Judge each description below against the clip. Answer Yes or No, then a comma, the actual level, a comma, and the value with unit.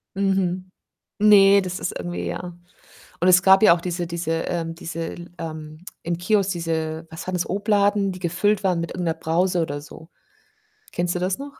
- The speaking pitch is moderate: Yes, medium, 175 Hz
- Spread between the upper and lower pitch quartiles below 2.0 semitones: No, narrow, 2.6 semitones